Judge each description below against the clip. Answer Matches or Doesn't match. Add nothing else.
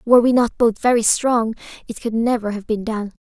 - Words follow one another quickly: Matches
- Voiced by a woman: Matches